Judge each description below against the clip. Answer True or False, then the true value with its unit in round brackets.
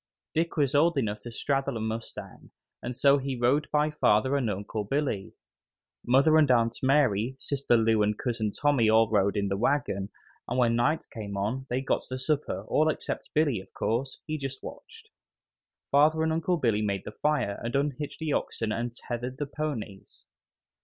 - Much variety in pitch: False (4.7 semitones)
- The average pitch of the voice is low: True (125 Hz)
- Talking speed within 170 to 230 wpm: True (180 wpm)